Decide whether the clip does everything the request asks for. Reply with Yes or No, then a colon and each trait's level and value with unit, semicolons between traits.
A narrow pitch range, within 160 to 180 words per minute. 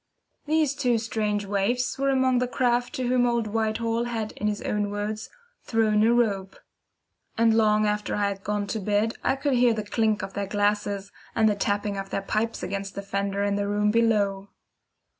No: narrow, 2.3 semitones; average, 195 wpm